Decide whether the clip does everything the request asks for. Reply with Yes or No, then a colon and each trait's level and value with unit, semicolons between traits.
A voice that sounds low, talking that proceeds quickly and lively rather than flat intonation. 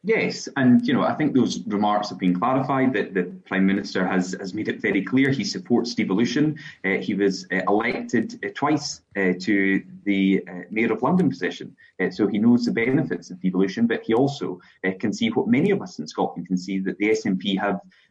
Yes: low, 100 Hz; fast, 215 wpm; wide, 5.8 semitones